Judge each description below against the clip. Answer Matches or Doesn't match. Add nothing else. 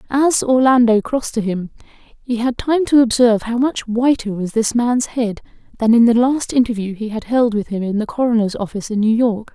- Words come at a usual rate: Doesn't match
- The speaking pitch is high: Matches